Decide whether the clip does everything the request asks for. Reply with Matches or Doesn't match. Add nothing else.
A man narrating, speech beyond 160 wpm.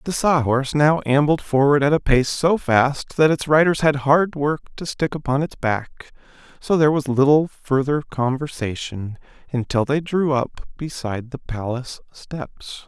Matches